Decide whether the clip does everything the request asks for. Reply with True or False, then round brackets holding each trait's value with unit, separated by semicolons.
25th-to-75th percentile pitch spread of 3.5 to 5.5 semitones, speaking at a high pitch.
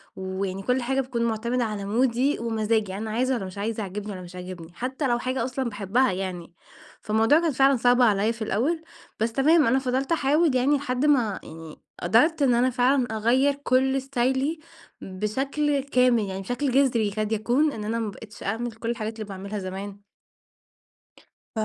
True (4.2 semitones; 235 Hz)